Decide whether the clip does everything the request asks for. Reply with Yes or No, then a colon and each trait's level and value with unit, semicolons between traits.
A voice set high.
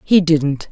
No: medium, 160 Hz